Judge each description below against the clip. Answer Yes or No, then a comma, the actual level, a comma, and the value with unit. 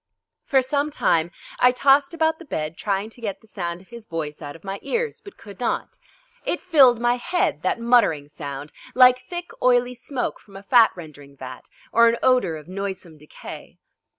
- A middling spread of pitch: No, wide, 7.4 semitones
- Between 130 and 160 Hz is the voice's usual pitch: No, high, 225 Hz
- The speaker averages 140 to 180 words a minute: No, average, 190 wpm